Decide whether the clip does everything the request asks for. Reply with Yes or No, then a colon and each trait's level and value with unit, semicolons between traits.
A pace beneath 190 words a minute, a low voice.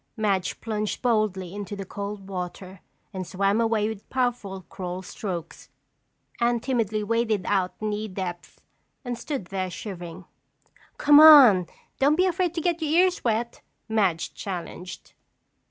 No: average, 140 wpm; high, 210 Hz